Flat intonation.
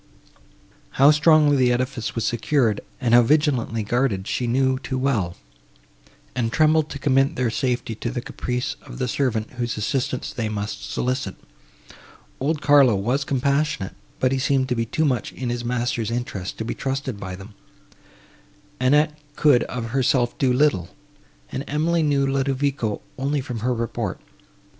No: average, 3.0 semitones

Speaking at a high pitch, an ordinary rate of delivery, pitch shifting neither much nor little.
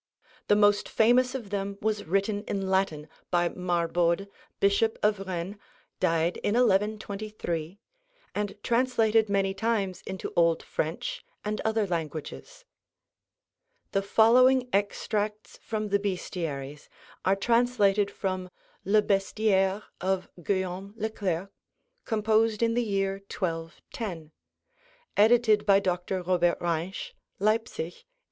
No: high, 200 Hz; slow, 115 wpm; average, 3.0 semitones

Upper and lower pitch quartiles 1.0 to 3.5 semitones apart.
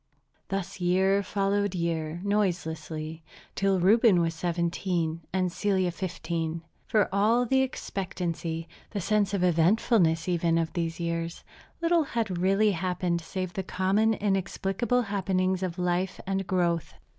Yes: average, 2.8 semitones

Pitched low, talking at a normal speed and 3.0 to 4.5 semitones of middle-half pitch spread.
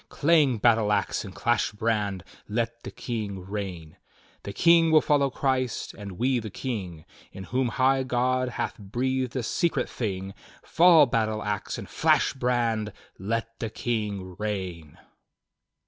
Yes: low, 115 Hz; average, 145 wpm; average, 4.1 semitones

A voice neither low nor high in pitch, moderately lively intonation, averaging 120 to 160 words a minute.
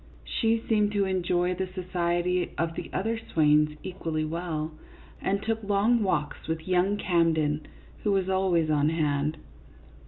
Yes: medium, 180 Hz; average, 3.7 semitones; average, 150 wpm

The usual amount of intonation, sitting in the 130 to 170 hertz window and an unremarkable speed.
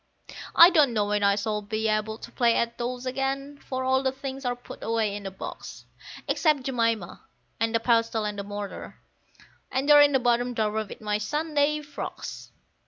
No: average, 3.9 semitones; high, 235 Hz; average, 185 wpm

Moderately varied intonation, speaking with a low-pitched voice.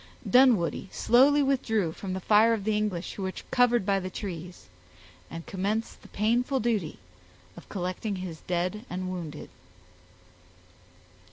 No: average, 3.9 semitones; high, 200 Hz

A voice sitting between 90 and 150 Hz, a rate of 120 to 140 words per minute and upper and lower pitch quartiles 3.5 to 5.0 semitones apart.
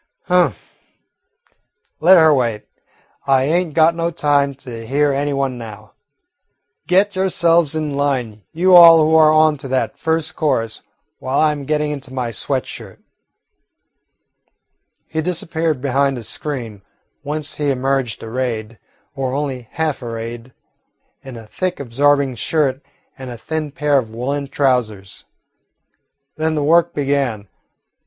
Yes: medium, 140 Hz; slow, 135 wpm; average, 3.8 semitones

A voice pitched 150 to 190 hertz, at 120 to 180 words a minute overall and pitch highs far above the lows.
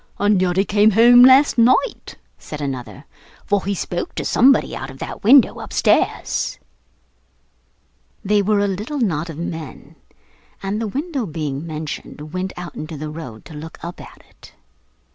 Yes: medium, 185 Hz; average, 160 wpm; wide, 5.9 semitones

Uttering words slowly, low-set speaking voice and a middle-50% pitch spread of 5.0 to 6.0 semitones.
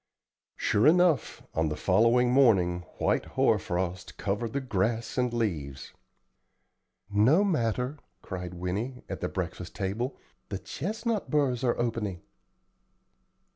Yes: slow, 120 wpm; low, 115 Hz; wide, 5.6 semitones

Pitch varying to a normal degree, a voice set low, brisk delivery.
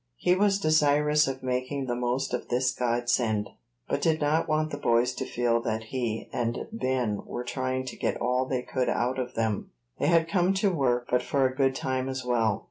Yes: average, 3.0 semitones; low, 130 Hz; fast, 210 wpm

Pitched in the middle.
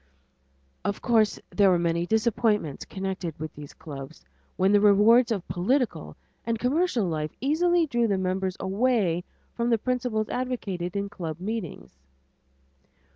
No: high, 205 Hz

